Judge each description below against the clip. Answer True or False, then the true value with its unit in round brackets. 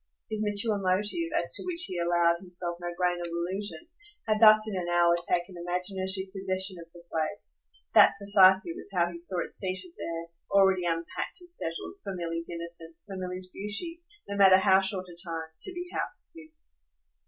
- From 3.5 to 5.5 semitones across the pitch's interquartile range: False (2.8 semitones)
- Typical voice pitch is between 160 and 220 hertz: True (185 Hz)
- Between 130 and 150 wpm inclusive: False (185 wpm)